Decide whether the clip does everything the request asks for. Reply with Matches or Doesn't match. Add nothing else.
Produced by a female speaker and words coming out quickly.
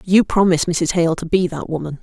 Matches